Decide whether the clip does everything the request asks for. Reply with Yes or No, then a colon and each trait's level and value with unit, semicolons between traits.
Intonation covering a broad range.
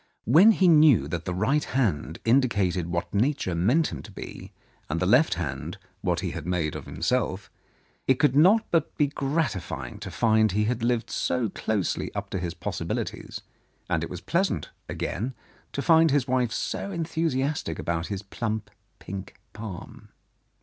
Yes: wide, 7.8 semitones